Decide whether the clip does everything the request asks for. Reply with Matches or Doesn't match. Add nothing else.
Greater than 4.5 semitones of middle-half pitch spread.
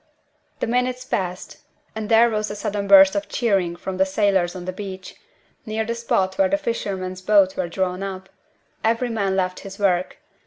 Doesn't match